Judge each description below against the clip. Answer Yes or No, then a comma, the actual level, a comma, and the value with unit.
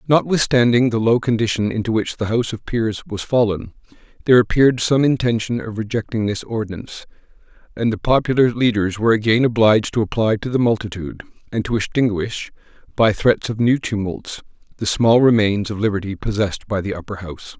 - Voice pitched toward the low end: Yes, low, 110 Hz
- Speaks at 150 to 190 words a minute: Yes, average, 170 wpm